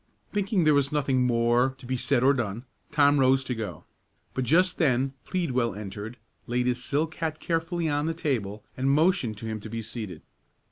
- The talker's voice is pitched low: Yes, low, 130 Hz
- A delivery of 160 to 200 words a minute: Yes, average, 190 wpm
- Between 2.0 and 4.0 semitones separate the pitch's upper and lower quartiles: No, average, 4.5 semitones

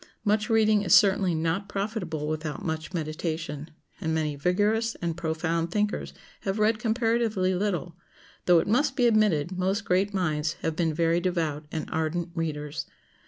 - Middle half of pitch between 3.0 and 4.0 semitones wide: No, average, 4.6 semitones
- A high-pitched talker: No, medium, 175 Hz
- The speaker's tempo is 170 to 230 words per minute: No, average, 155 wpm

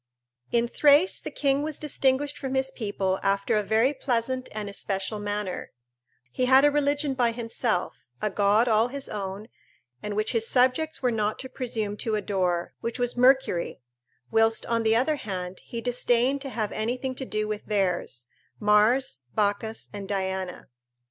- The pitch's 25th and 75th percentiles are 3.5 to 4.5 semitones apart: Yes, average, 4.1 semitones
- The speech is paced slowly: No, average, 165 wpm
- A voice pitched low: No, high, 225 Hz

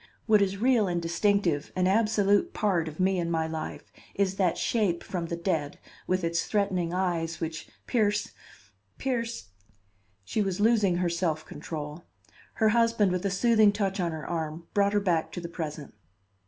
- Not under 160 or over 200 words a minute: Yes, average, 175 wpm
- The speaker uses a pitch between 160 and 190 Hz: Yes, medium, 185 Hz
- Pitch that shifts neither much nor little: Yes, average, 3.7 semitones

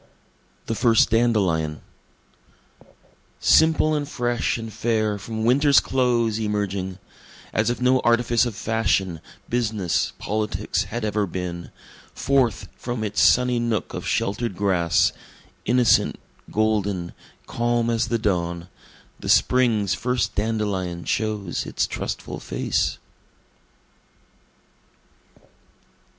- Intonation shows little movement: No, average, 3.4 semitones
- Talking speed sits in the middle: No, slow, 105 wpm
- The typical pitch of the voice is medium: No, low, 110 Hz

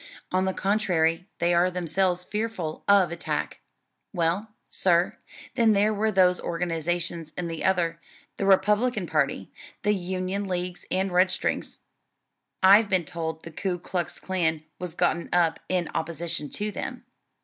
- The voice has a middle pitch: Yes, medium, 180 Hz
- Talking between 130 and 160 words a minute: Yes, average, 140 wpm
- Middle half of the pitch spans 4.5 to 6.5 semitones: No, narrow, 2.5 semitones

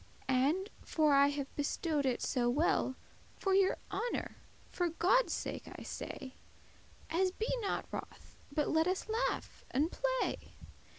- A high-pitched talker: Yes, very high, 320 Hz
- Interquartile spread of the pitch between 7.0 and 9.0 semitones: No, average, 5.2 semitones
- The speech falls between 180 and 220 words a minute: No, average, 140 wpm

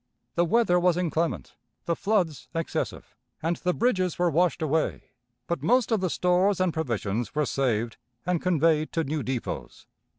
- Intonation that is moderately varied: Yes, average, 3.3 semitones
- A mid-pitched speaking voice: Yes, medium, 170 Hz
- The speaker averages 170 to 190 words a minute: No, average, 160 wpm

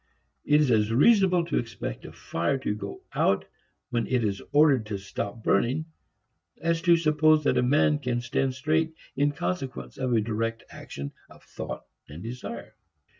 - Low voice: Yes, low, 130 Hz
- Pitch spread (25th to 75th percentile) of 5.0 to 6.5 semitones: Yes, wide, 5.4 semitones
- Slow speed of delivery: No, average, 170 wpm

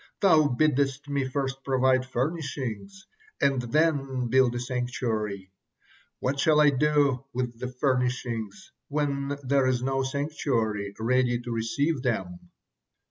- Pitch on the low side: Yes, low, 130 Hz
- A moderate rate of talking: No, slow, 125 wpm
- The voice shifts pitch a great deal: No, narrow, 2.6 semitones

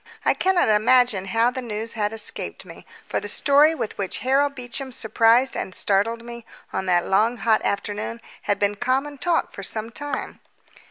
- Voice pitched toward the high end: Yes, high, 230 Hz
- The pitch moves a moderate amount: Yes, average, 3.9 semitones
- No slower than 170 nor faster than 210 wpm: Yes, average, 175 wpm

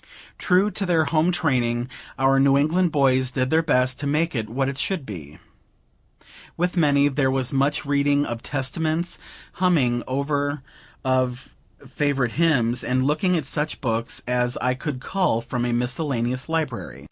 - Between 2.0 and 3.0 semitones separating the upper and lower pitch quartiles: No, average, 3.7 semitones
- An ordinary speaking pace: Yes, average, 160 wpm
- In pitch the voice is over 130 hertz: Yes, medium, 140 Hz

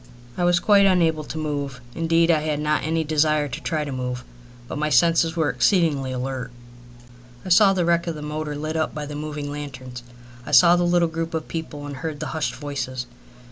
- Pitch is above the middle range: No, medium, 155 Hz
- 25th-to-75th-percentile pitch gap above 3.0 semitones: No, narrow, 2.4 semitones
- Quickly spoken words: Yes, fast, 210 wpm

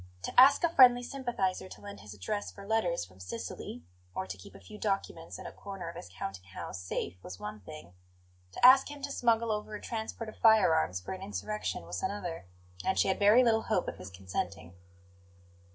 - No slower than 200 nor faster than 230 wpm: Yes, fast, 205 wpm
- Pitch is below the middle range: No, high, 195 Hz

